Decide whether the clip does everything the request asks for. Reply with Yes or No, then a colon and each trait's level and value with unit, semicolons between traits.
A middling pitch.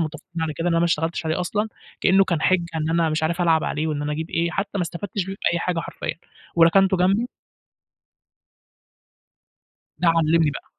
Yes: medium, 170 Hz